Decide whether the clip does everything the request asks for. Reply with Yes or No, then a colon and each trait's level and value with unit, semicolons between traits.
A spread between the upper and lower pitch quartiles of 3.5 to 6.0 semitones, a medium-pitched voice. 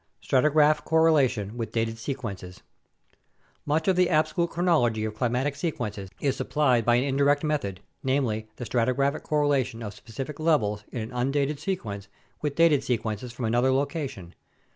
No: average, 4.9 semitones; low, 130 Hz